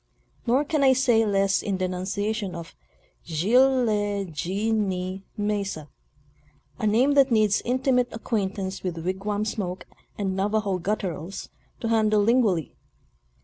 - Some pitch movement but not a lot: Yes, average, 3.2 semitones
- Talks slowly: Yes, slow, 130 wpm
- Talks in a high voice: Yes, high, 205 Hz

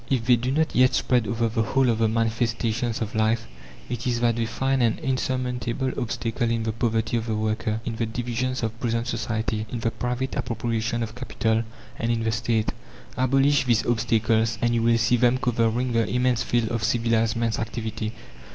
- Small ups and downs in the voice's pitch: Yes, narrow, 1.6 semitones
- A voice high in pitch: No, low, 115 Hz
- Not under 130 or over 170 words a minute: No, average, 195 wpm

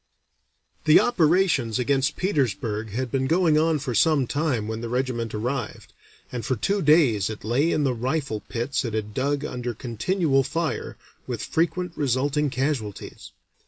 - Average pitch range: Yes, average, 4.8 semitones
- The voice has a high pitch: No, low, 135 Hz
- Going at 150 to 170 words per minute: Yes, average, 155 wpm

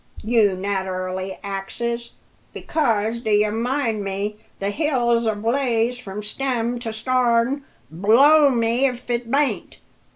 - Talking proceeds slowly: Yes, slow, 120 wpm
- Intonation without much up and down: No, average, 3.2 semitones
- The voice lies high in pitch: Yes, high, 230 Hz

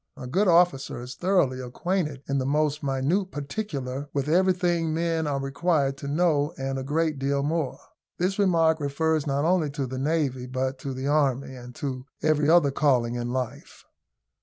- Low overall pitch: No, medium, 145 Hz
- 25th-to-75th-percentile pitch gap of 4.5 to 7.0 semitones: No, average, 3.6 semitones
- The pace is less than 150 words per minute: No, average, 175 wpm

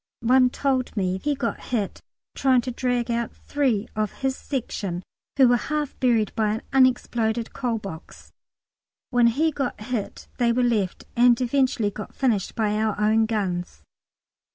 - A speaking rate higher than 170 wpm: No, average, 155 wpm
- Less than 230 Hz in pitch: No, high, 235 Hz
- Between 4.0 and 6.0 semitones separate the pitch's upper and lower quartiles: No, average, 3.2 semitones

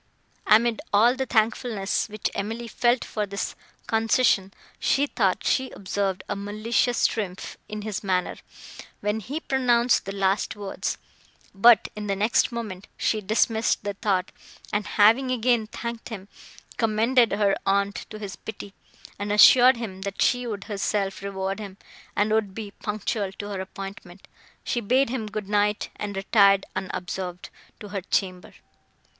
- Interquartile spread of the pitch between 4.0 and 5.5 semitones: No, narrow, 2.6 semitones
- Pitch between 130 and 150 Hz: No, high, 210 Hz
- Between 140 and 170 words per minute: Yes, average, 150 wpm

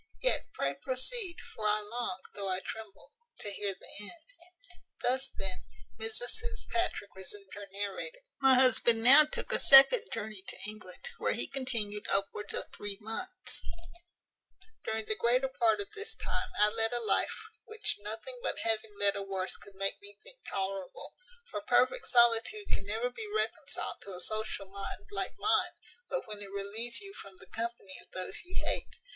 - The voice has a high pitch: Yes, high, 225 Hz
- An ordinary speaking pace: Yes, average, 175 wpm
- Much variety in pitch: Yes, wide, 8.8 semitones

